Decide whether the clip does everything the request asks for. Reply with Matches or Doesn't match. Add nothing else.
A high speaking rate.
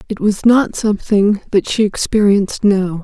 Doesn't match